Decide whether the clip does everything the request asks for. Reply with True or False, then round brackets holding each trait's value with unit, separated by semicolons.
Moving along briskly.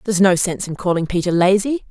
True (220 wpm)